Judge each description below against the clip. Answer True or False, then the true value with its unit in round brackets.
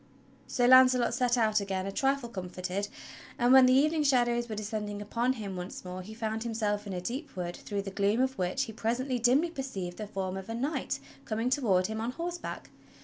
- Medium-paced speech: False (215 wpm)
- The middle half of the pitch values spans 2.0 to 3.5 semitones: False (4.3 semitones)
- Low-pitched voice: False (225 Hz)